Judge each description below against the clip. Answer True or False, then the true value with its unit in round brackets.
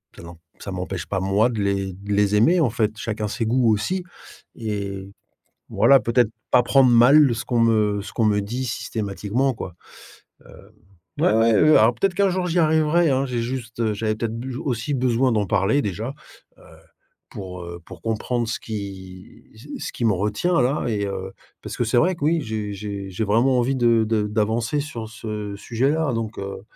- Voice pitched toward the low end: True (115 Hz)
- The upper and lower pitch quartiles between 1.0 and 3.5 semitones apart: False (3.9 semitones)